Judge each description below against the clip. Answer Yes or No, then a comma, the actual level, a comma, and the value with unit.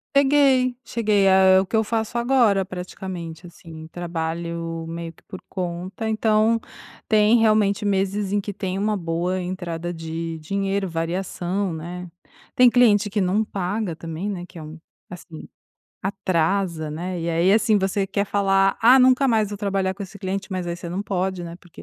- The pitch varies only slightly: No, average, 3.3 semitones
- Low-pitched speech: No, high, 190 Hz